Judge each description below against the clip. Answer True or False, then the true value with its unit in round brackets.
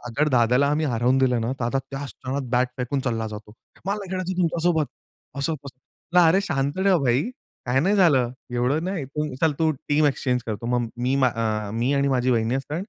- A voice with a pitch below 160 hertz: True (135 Hz)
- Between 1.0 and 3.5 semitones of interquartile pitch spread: False (4.1 semitones)